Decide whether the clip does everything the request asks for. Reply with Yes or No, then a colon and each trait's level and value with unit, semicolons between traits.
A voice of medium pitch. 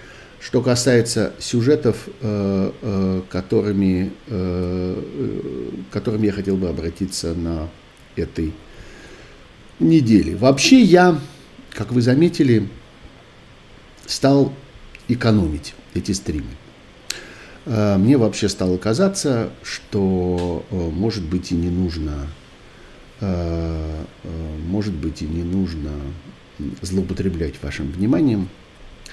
No: very low, 95 Hz